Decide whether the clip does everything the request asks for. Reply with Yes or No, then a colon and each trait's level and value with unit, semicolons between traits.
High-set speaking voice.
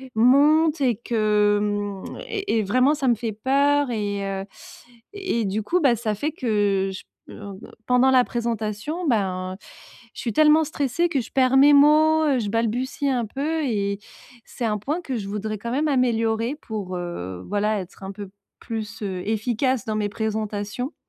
Yes: high, 230 Hz